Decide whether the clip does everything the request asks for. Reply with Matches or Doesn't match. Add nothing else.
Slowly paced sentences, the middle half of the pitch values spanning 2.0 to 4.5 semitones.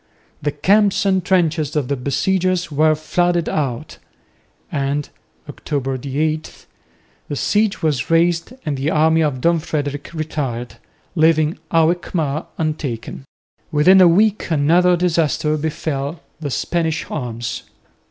Matches